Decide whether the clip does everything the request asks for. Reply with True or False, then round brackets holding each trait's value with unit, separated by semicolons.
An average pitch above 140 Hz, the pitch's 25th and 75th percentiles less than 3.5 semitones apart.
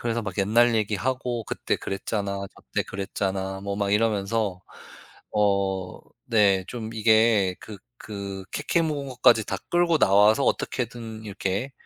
False (105 Hz; 3.1 semitones)